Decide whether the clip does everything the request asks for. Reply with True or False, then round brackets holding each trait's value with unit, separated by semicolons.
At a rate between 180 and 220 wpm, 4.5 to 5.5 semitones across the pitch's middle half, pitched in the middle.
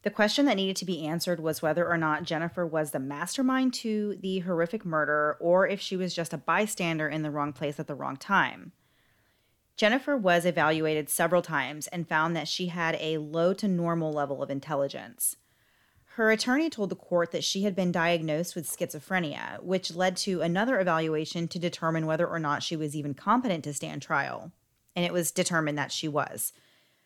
False (195 wpm; 3.3 semitones; 170 Hz)